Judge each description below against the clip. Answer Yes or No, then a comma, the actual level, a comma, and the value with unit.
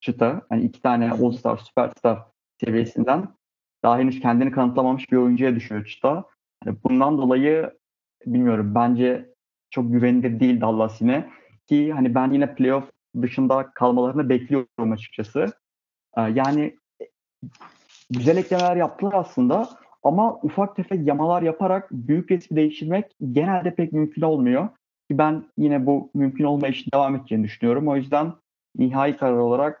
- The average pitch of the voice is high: No, low, 135 Hz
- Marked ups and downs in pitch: No, average, 4.4 semitones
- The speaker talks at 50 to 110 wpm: No, average, 135 wpm